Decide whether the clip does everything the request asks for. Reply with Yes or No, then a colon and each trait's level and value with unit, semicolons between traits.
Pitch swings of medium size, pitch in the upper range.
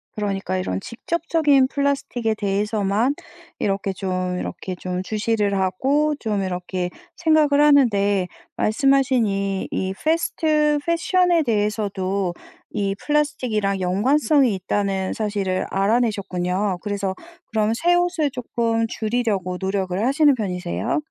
No: wide, 6.2 semitones; high, 210 Hz